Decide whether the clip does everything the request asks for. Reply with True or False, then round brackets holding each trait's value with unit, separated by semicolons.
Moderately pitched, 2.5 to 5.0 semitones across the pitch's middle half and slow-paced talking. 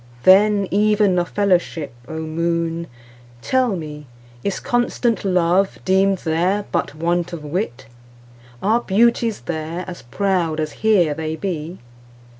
True (175 Hz; 4.2 semitones; 115 wpm)